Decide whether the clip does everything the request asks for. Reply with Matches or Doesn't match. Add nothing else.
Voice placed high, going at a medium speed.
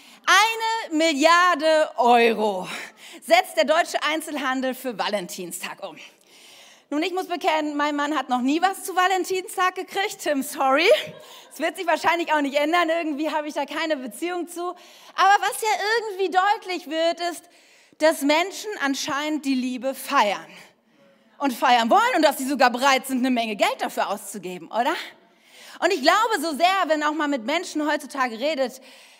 Matches